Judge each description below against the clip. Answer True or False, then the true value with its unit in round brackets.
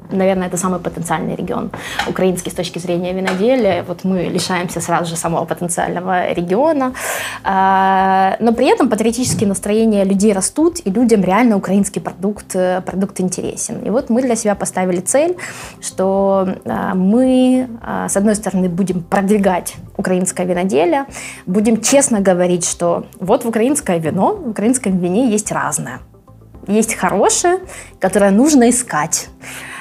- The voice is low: False (195 Hz)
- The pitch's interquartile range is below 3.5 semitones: False (3.8 semitones)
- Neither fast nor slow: True (135 wpm)